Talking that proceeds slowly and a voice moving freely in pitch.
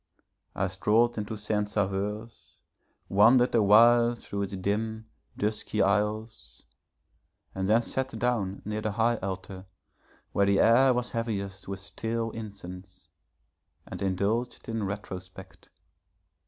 No: slow, 120 wpm; narrow, 2.6 semitones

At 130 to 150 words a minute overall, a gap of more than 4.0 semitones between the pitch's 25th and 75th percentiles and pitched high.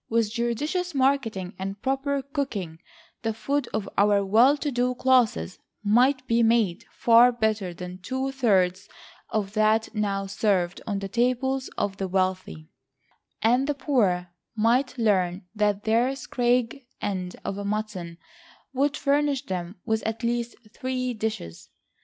Yes: average, 140 wpm; average, 4.7 semitones; high, 225 Hz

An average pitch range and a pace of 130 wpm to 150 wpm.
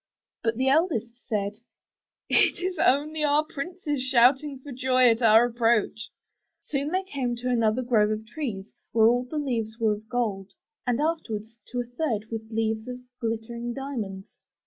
No: average, 3.9 semitones; average, 170 wpm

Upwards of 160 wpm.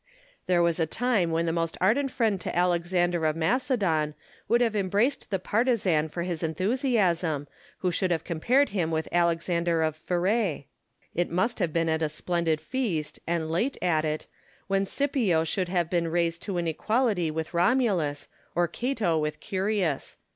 Yes: average, 170 wpm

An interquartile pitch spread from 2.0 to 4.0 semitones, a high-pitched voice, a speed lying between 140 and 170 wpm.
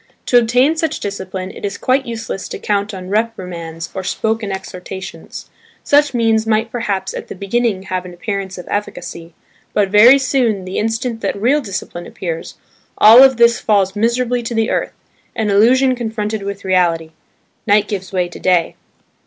Yes: average, 3.7 semitones; high, 210 Hz; average, 165 wpm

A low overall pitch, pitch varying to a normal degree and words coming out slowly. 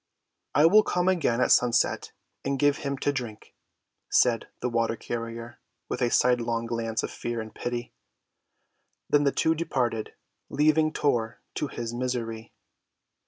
No: low, 120 Hz; average, 3.7 semitones; average, 145 wpm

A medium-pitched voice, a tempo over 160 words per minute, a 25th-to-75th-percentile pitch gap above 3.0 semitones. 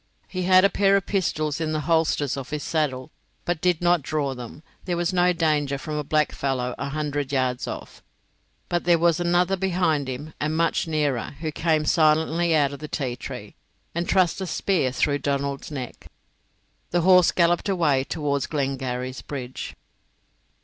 Yes: medium, 155 Hz; average, 175 wpm; average, 3.7 semitones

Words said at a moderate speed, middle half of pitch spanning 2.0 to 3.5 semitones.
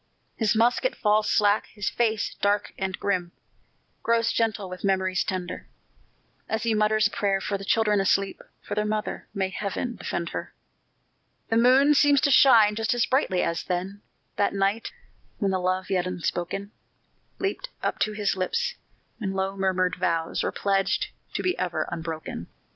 Yes: average, 165 wpm; average, 2.9 semitones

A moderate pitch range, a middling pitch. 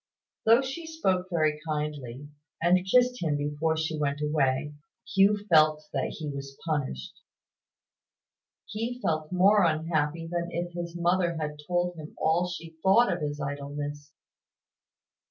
Yes: average, 3.2 semitones; medium, 160 Hz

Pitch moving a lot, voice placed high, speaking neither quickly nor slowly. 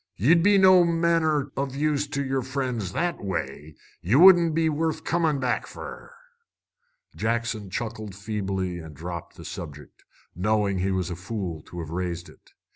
No: wide, 8.9 semitones; low, 115 Hz; average, 160 wpm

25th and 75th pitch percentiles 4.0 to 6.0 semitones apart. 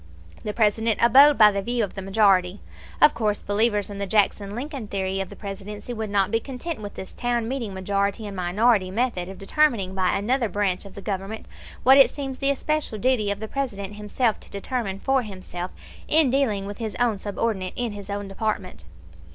No: average, 3.5 semitones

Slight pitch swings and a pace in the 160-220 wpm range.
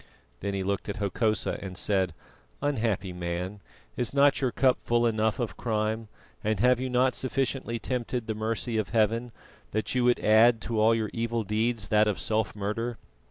Yes: narrow, 2.3 semitones; average, 180 wpm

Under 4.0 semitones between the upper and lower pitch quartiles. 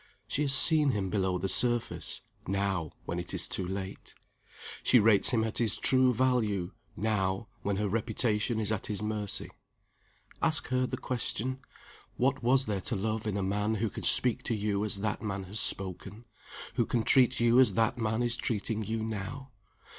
Yes: average, 3.4 semitones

